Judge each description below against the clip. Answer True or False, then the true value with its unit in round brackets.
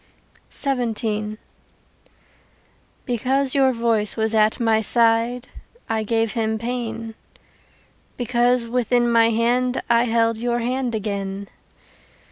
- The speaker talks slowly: True (100 wpm)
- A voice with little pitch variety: True (1.9 semitones)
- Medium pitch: False (230 Hz)